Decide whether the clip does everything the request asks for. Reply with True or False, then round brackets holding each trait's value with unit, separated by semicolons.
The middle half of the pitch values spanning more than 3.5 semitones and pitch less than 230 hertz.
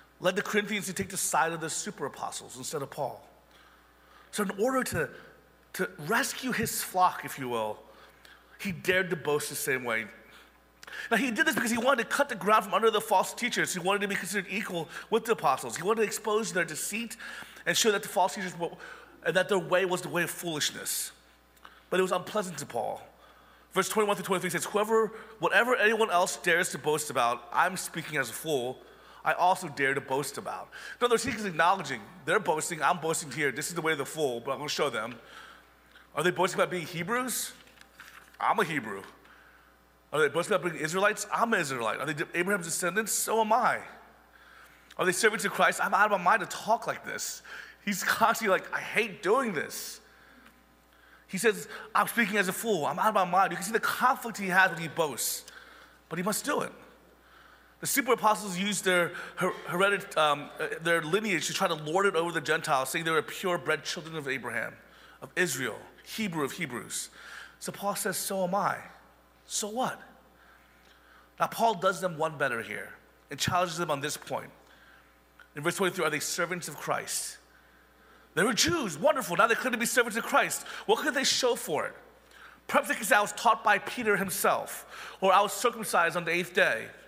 True (5.1 semitones; 185 Hz)